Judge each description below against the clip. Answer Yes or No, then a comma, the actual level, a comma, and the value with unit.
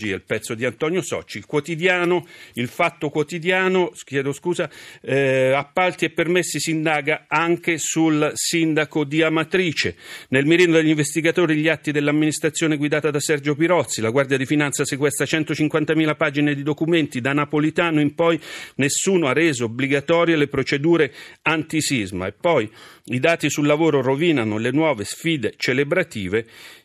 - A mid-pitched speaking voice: Yes, medium, 155 Hz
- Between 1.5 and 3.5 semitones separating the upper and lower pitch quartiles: Yes, average, 2.7 semitones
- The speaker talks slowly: No, average, 145 wpm